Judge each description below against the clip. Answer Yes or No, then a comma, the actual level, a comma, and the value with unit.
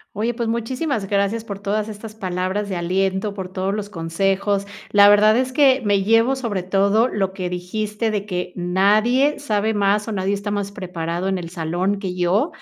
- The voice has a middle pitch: No, high, 200 Hz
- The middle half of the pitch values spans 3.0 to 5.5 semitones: No, narrow, 2.5 semitones